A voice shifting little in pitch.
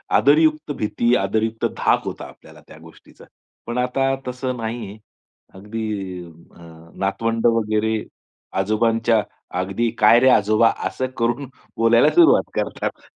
Yes: narrow, 2.3 semitones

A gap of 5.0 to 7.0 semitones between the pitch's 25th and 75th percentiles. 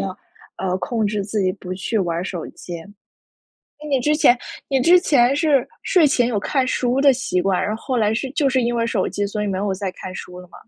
Yes: wide, 5.6 semitones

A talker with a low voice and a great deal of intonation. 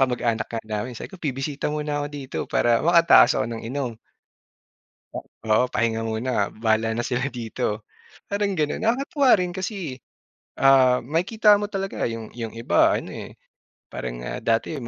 Yes: low, 130 Hz; wide, 6.6 semitones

